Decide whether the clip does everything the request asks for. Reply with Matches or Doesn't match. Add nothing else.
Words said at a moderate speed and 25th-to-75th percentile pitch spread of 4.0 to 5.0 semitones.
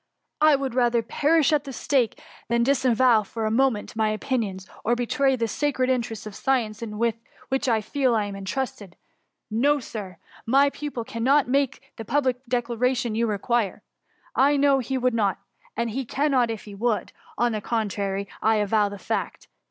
Doesn't match